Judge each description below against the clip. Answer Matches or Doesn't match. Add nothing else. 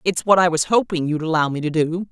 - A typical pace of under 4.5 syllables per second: Doesn't match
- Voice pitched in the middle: Matches